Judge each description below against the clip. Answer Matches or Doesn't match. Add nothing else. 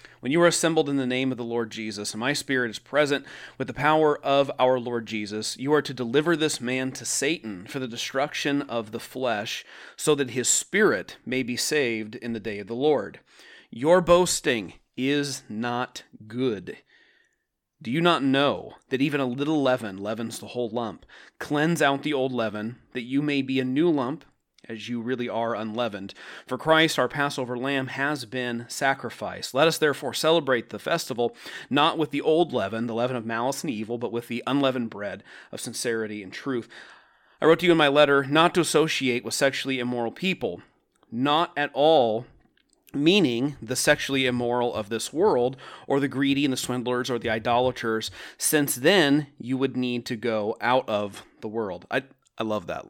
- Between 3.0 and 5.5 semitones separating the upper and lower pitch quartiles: Matches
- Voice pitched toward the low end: Matches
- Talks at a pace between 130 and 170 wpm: Doesn't match